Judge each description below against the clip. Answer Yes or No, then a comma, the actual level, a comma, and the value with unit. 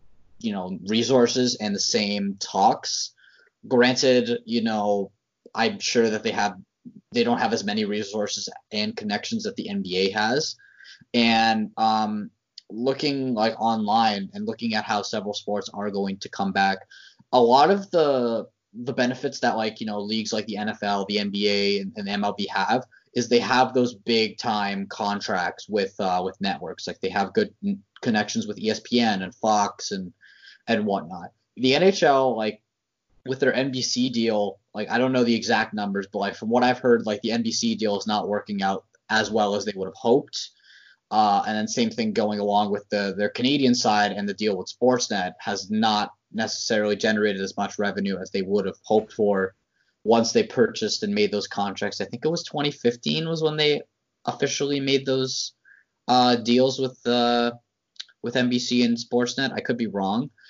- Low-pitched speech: Yes, low, 115 Hz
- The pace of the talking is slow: No, average, 180 wpm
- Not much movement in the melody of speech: No, average, 3.8 semitones